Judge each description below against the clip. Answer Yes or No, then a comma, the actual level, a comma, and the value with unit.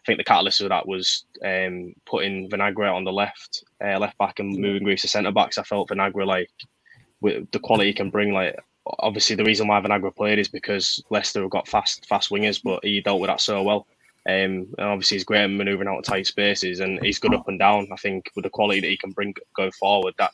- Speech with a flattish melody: Yes, narrow, 1.3 semitones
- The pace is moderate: No, fast, 245 wpm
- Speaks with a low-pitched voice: Yes, low, 100 Hz